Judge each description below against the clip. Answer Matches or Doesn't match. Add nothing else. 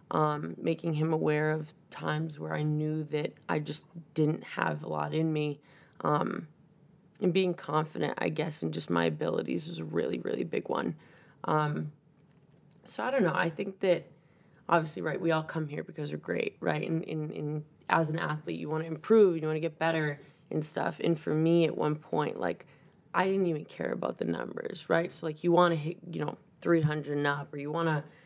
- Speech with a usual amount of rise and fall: Doesn't match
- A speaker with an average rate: Doesn't match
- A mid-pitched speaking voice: Matches